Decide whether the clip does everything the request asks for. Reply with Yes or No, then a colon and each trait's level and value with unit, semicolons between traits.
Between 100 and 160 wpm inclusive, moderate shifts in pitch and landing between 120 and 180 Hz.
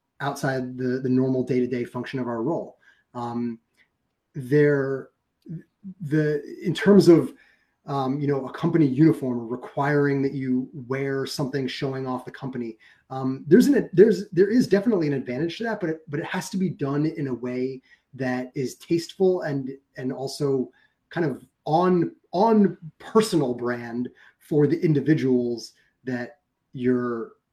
Yes: average, 155 wpm; average, 3.9 semitones; low, 135 Hz